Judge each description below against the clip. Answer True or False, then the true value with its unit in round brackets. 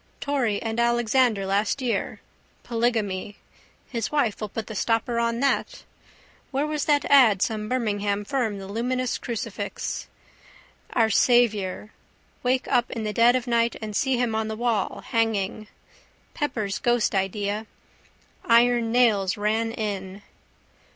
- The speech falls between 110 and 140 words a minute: True (135 wpm)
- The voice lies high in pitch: True (225 Hz)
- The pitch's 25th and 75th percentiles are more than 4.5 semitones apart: False (2.7 semitones)